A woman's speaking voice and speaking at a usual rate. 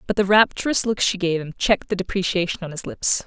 No: female; fast, 240 wpm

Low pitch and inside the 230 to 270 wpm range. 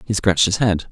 Yes: low, 100 Hz; fast, 260 wpm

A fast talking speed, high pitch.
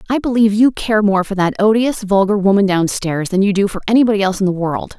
Yes: fast, 255 wpm; high, 200 Hz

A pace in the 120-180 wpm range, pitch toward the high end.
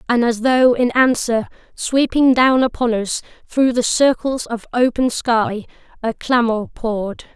Yes: average, 145 wpm; high, 240 Hz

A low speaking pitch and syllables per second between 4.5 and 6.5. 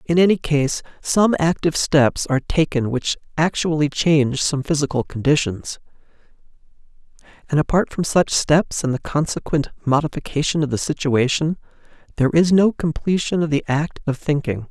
No: medium, 150 Hz; 5.1 syllables/s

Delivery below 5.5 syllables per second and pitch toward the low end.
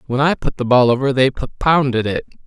No: 5.9 syllables/s; low, 130 Hz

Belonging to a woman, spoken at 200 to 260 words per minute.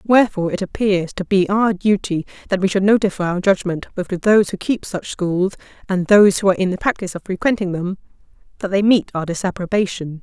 Yes: female; fast, 205 wpm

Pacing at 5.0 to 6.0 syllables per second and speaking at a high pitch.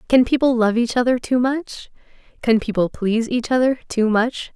Yes: 5.1 syllables/s; high, 240 Hz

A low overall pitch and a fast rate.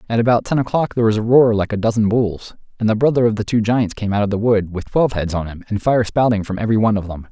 Yes: low, 110 Hz; fast, 305 wpm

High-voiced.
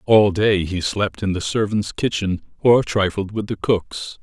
No: low, 100 Hz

